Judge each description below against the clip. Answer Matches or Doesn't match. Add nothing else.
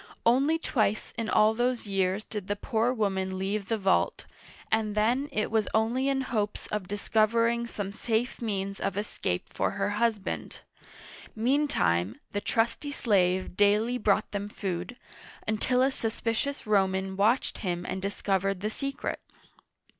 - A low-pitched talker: Doesn't match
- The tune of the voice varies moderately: Matches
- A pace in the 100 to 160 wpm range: Matches